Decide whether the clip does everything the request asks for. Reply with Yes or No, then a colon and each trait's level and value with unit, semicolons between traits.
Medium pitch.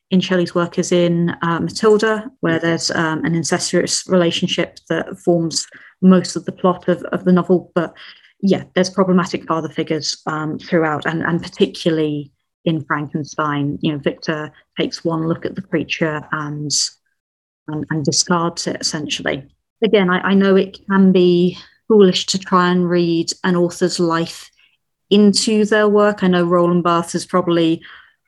Yes: medium, 175 Hz